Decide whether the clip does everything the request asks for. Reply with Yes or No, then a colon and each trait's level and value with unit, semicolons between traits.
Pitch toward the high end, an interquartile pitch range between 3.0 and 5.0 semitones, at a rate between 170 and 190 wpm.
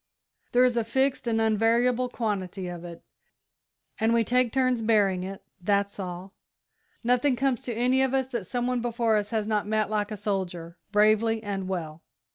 Yes: high, 220 Hz; average, 3.6 semitones; average, 180 wpm